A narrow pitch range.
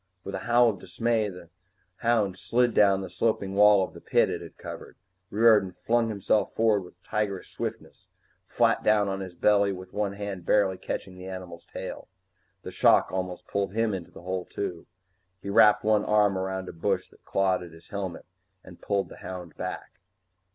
Yes: narrow, 2.3 semitones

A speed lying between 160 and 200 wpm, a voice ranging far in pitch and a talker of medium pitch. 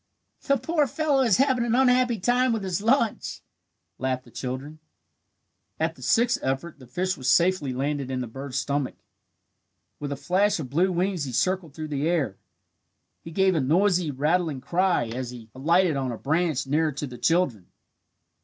Yes: average, 175 wpm; wide, 6.3 semitones; medium, 160 Hz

